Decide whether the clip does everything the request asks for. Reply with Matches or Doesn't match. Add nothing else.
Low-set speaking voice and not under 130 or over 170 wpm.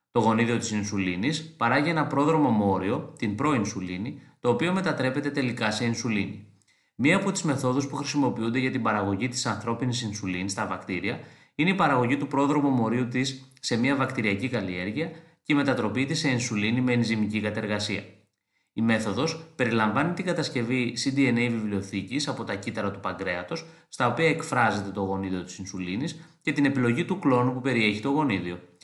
Matches